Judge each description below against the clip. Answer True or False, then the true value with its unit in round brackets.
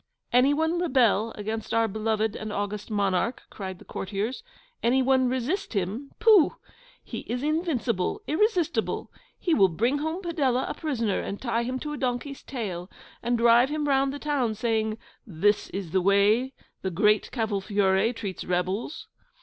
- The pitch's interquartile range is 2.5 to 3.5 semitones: False (5.3 semitones)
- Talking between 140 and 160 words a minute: True (155 wpm)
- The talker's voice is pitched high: True (235 Hz)